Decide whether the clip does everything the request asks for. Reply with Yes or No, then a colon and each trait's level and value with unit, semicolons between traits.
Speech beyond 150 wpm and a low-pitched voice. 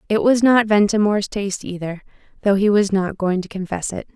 No: average, 200 wpm; high, 200 Hz